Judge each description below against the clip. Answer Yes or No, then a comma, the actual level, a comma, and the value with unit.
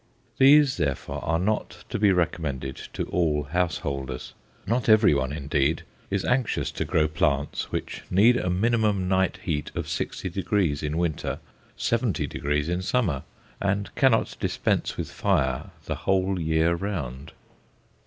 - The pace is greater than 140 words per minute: No, slow, 135 wpm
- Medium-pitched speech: No, very low, 85 Hz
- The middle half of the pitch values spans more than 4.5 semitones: Yes, average, 5.3 semitones